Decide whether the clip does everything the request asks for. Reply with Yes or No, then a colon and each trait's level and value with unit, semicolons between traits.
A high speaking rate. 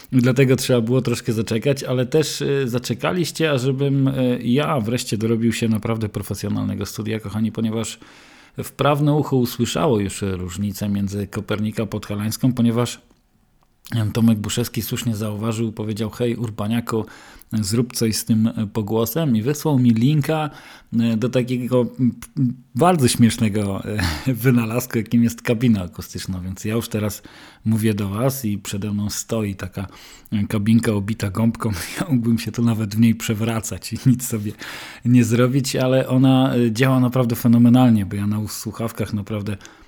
No: average, 140 wpm